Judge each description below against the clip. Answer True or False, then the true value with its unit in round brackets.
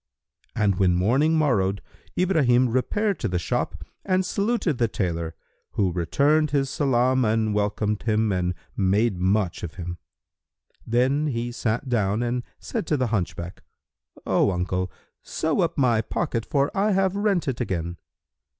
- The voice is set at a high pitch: False (120 Hz)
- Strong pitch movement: True (7.2 semitones)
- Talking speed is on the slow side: False (150 wpm)